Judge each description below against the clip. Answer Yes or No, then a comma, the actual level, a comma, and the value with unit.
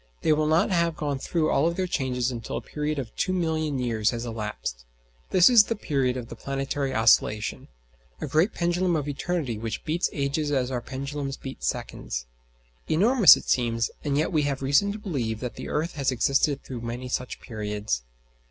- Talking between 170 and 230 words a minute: Yes, average, 185 wpm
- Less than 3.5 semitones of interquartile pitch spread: No, average, 4.6 semitones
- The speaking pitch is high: No, medium, 140 Hz